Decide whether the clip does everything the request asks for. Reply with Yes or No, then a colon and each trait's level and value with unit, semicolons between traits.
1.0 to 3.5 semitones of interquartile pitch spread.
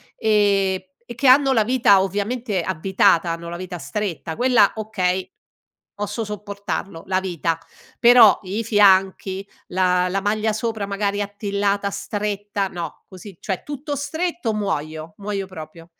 Yes: narrow, 2.4 semitones